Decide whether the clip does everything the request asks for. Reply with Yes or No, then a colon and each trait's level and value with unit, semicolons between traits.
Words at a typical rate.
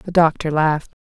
Yes: average, 175 wpm